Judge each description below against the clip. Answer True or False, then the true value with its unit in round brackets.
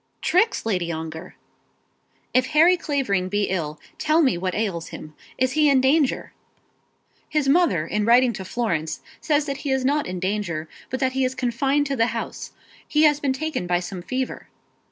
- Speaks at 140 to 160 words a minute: False (180 wpm)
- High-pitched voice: True (255 Hz)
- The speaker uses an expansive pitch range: True (7.6 semitones)